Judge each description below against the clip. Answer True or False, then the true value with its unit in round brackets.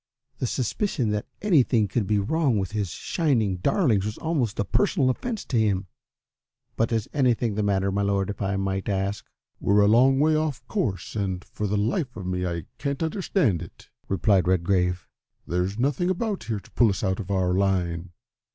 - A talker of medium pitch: False (105 Hz)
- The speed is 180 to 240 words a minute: True (190 wpm)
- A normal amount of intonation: False (5.7 semitones)